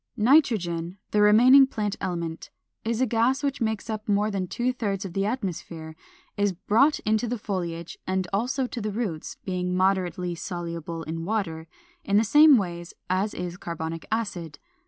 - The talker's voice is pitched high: Yes, high, 200 Hz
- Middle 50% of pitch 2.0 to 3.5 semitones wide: No, average, 4.6 semitones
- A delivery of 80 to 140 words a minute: No, average, 165 wpm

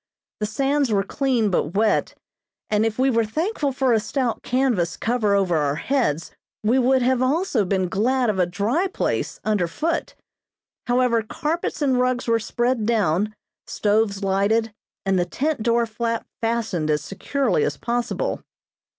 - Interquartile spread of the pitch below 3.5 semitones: No, average, 4.5 semitones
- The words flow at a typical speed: Yes, average, 160 wpm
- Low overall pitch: No, high, 230 Hz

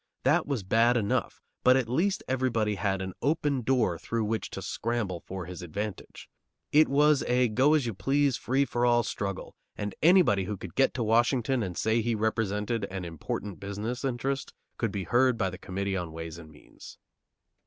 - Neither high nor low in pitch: No, low, 115 Hz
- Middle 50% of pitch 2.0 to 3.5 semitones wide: No, average, 4.8 semitones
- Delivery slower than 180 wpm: No, average, 185 wpm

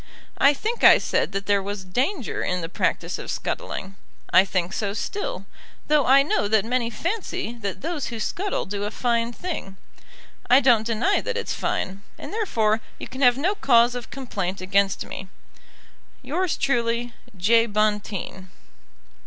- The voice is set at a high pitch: Yes, high, 230 Hz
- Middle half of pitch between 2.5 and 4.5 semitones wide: No, wide, 5.5 semitones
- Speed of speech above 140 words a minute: Yes, average, 160 wpm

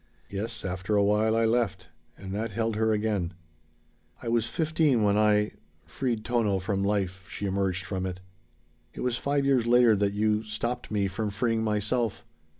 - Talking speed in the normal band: Yes, average, 170 wpm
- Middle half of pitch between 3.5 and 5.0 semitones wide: No, narrow, 2.6 semitones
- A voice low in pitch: Yes, low, 105 Hz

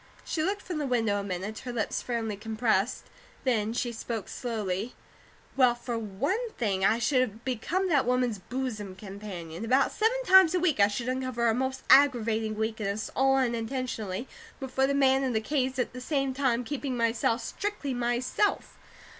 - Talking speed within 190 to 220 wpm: No, average, 170 wpm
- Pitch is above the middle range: Yes, high, 245 Hz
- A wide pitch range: No, average, 3.5 semitones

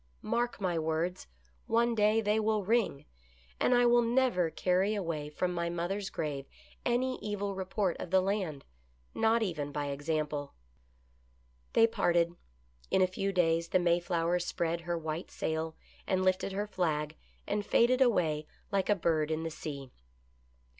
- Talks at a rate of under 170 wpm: Yes, average, 155 wpm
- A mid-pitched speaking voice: Yes, medium, 180 Hz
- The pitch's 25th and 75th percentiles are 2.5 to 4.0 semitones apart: No, average, 4.4 semitones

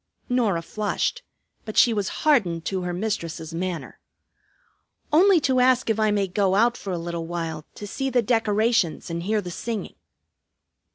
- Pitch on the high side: Yes, high, 205 Hz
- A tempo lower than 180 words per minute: Yes, average, 165 wpm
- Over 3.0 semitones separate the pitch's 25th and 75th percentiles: Yes, average, 5.2 semitones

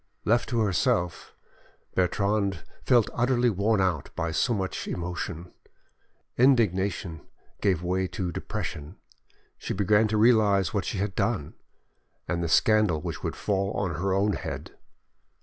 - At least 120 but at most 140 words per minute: Yes, slow, 135 wpm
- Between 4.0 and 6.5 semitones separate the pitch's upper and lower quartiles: No, average, 3.4 semitones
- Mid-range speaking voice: No, very low, 95 Hz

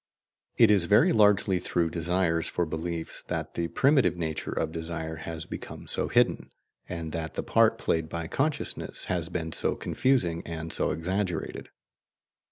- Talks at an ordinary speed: Yes, average, 155 wpm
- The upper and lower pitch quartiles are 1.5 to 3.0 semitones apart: Yes, narrow, 2.5 semitones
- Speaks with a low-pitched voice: Yes, very low, 85 Hz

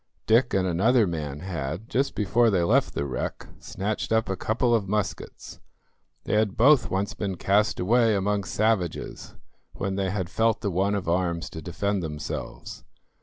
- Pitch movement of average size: Yes, average, 3.6 semitones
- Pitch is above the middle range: No, low, 100 Hz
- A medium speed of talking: Yes, average, 170 wpm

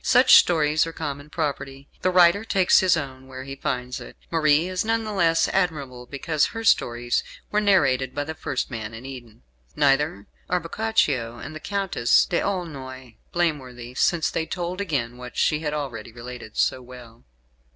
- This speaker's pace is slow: No, average, 170 wpm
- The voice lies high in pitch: No, medium, 145 Hz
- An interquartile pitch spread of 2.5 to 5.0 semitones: No, wide, 5.5 semitones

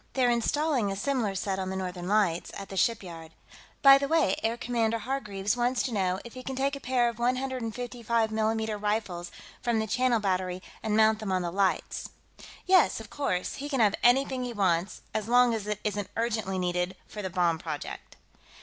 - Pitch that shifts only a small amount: No, average, 4.3 semitones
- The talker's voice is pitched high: Yes, high, 220 Hz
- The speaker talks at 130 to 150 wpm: No, average, 195 wpm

